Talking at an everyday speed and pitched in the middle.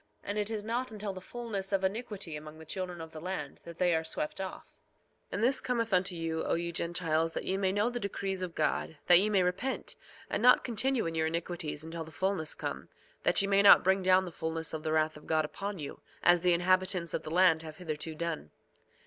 No: fast, 235 wpm; medium, 180 Hz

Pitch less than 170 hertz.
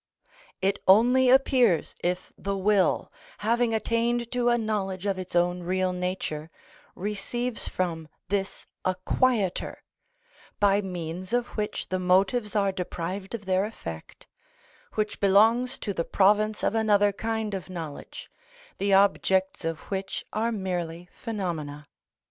No: high, 195 Hz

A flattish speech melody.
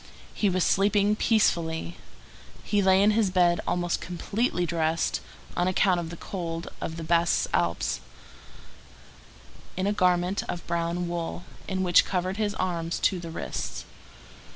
Yes: narrow, 2.3 semitones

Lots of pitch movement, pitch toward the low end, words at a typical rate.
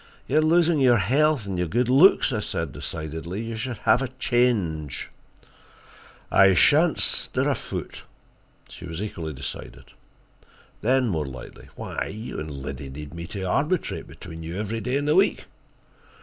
Yes: wide, 8.2 semitones; low, 105 Hz; average, 165 wpm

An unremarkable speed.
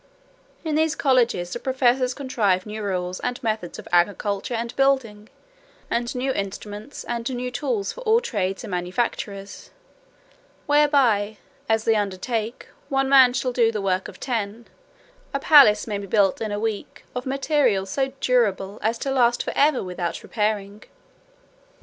Yes: average, 150 wpm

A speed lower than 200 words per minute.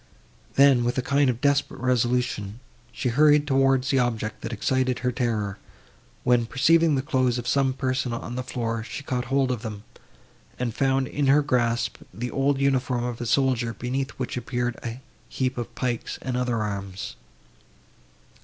Yes: average, 170 wpm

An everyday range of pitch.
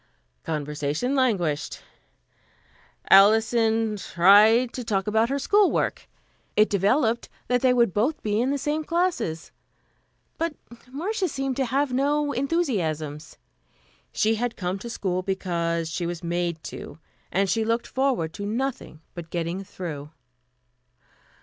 No: wide, 7.1 semitones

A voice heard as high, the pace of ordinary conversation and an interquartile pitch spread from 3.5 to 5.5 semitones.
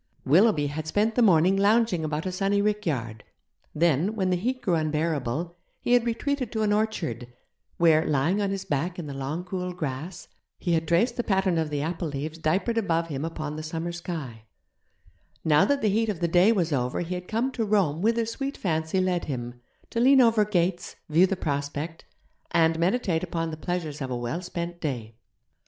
No: medium, 170 Hz; average, 195 wpm; average, 4.6 semitones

